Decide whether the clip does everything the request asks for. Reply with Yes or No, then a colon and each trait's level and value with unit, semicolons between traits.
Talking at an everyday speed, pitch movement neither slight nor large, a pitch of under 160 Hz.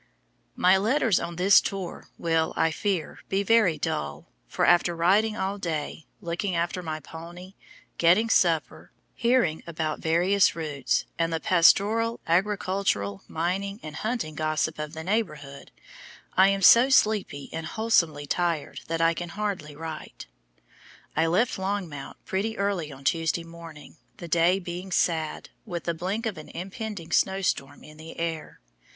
No: average, 150 wpm; average, 3.6 semitones; medium, 170 Hz